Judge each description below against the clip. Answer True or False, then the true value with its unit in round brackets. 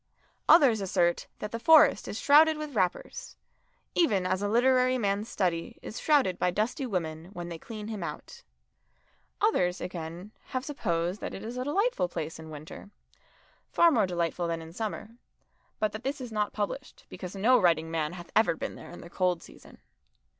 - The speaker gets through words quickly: False (180 wpm)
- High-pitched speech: True (200 Hz)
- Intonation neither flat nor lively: False (6.3 semitones)